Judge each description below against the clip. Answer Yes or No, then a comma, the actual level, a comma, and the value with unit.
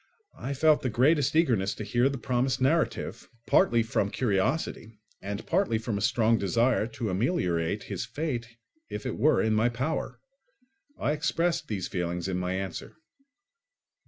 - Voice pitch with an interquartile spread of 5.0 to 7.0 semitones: Yes, wide, 5.6 semitones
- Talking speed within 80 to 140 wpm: No, average, 155 wpm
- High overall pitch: No, low, 115 Hz